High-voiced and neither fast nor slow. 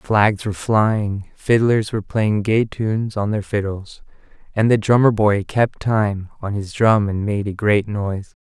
No: low, 105 Hz; average, 175 wpm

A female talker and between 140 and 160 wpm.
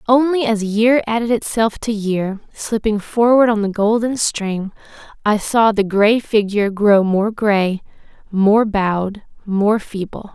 Yes: female; average, 145 wpm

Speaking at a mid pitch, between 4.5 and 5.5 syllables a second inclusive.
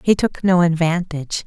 Yes: medium, 170 Hz; 5.1 syllables/s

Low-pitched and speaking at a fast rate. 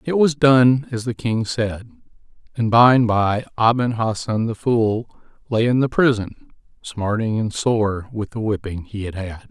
No: low, 115 Hz; average, 175 wpm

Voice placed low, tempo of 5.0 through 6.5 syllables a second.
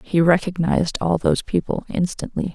No: medium, 175 Hz; 5.4 syllables/s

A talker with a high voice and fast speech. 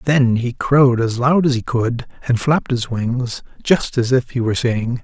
No: low, 125 Hz; fast, 215 wpm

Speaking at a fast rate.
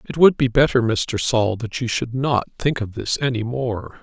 Yes: fast, 225 wpm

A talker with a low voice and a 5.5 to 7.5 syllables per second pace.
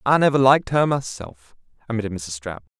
Yes: low, 120 Hz; 6.0 syllables/s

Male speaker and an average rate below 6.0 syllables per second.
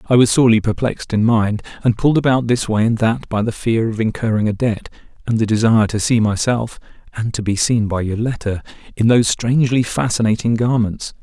Yes: male; 5.3 syllables/s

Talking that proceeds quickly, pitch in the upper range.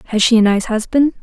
Yes: fast, 245 wpm; high, 230 Hz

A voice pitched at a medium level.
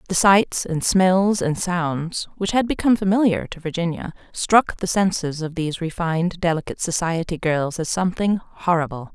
Yes: medium, 175 Hz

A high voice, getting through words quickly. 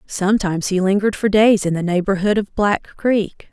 No: high, 200 Hz; average, 190 wpm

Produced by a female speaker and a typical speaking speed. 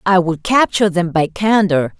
Yes: female; average, 180 wpm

